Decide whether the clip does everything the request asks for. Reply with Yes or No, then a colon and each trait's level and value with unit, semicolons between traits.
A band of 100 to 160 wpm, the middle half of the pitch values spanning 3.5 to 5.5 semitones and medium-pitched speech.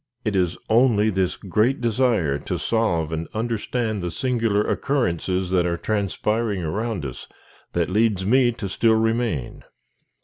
No: average, 140 wpm; average, 4.4 semitones; low, 105 Hz